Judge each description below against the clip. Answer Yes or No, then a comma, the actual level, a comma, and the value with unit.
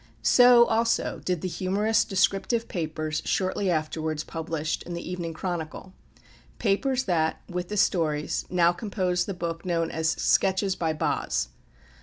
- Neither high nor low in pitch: Yes, medium, 180 Hz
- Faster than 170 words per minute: No, average, 140 wpm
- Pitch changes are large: No, average, 3.3 semitones